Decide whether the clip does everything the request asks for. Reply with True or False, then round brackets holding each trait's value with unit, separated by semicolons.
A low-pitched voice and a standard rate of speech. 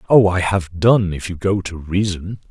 False (95 Hz; 215 wpm)